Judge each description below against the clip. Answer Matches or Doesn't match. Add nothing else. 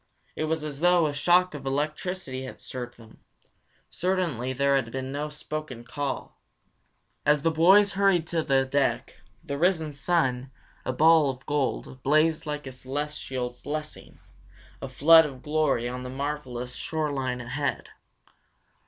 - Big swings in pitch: Doesn't match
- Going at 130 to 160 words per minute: Matches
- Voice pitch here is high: Doesn't match